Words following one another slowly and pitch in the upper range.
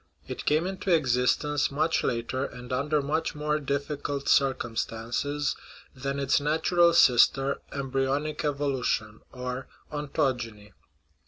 No: slow, 105 wpm; medium, 140 Hz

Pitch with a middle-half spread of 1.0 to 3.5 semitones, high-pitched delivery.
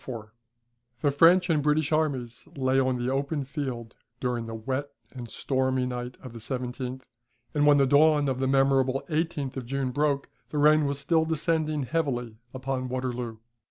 No: average, 2.9 semitones; low, 135 Hz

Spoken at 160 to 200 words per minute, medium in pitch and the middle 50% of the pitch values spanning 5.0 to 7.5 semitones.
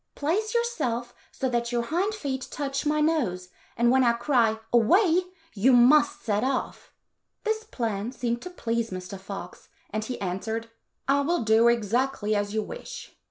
No: average, 175 wpm; high, 245 Hz; wide, 5.4 semitones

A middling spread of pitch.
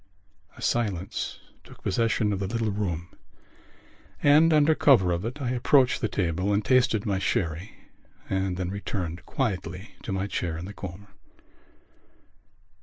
Yes: average, 4.4 semitones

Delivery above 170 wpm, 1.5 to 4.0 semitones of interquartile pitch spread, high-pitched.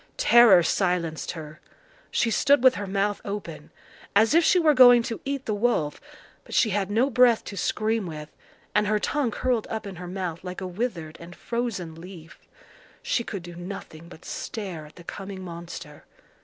No: average, 185 wpm; average, 5.3 semitones; high, 200 Hz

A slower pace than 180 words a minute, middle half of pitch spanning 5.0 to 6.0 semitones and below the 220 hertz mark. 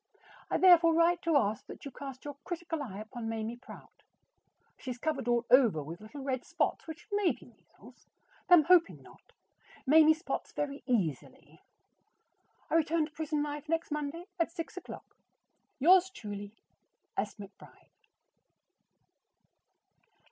No: average, 150 wpm; wide, 5.6 semitones; very high, 290 Hz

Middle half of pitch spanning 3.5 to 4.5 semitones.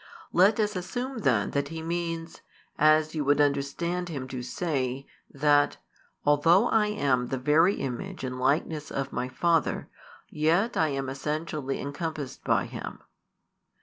Yes: average, 3.9 semitones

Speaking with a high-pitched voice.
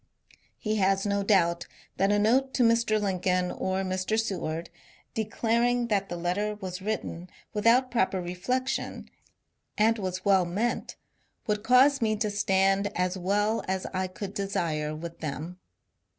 Yes: high, 195 Hz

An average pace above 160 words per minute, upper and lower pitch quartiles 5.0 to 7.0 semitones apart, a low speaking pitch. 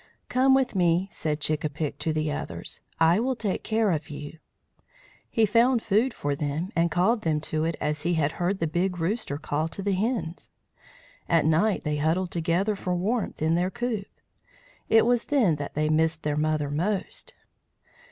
No: average, 185 wpm; average, 5.3 semitones; medium, 170 Hz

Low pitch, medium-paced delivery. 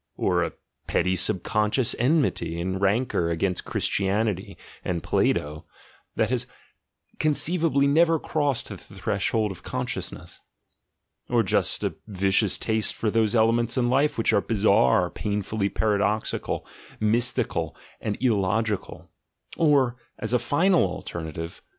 No: low, 110 Hz; slow, 120 wpm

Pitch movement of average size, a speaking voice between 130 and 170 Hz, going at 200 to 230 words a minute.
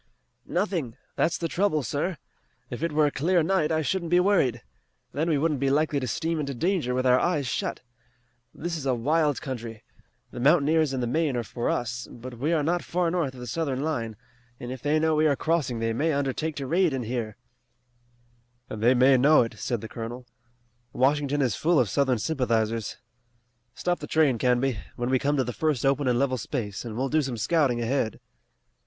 Yes: average, 4.4 semitones; medium, 140 Hz; fast, 205 wpm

